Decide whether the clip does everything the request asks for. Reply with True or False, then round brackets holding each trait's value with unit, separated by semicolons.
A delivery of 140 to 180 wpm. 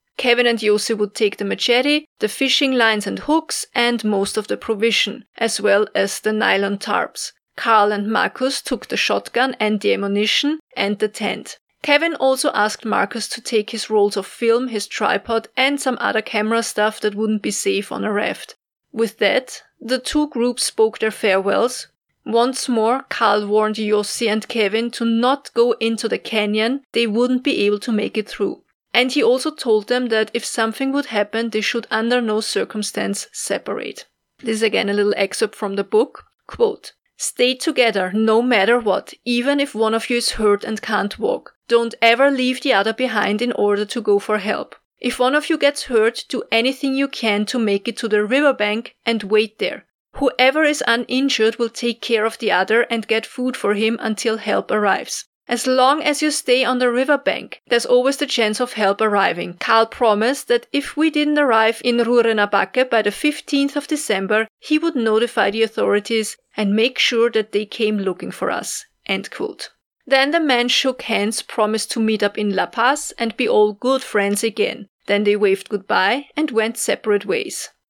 False (190 wpm)